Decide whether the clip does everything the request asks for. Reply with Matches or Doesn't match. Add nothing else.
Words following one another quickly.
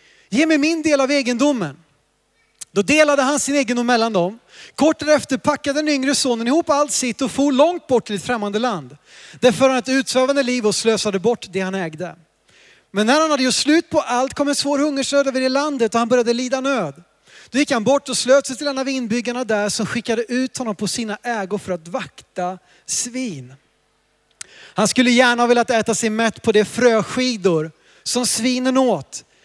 Matches